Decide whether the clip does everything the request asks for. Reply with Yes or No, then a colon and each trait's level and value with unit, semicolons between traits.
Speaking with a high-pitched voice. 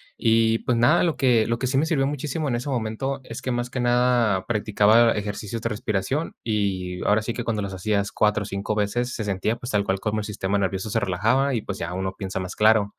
No: low, 110 Hz